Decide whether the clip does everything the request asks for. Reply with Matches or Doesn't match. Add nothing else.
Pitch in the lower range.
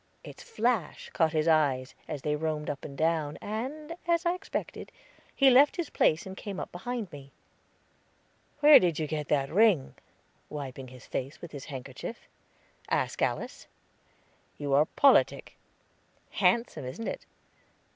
Doesn't match